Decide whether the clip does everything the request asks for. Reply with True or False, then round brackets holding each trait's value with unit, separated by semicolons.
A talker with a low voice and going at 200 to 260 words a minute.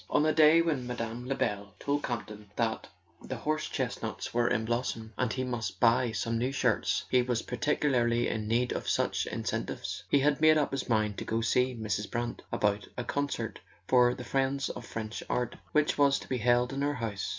True (125 Hz; 205 wpm)